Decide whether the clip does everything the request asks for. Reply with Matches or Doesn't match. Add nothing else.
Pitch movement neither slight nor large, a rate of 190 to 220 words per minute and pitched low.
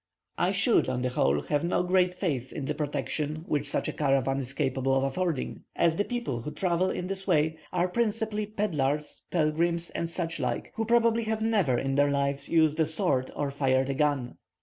Doesn't match